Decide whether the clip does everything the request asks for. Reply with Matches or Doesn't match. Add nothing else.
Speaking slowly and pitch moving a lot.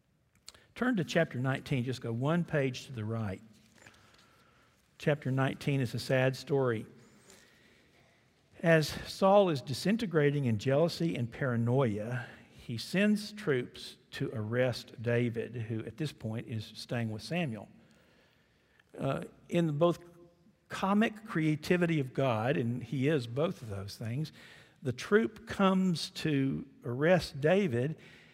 Matches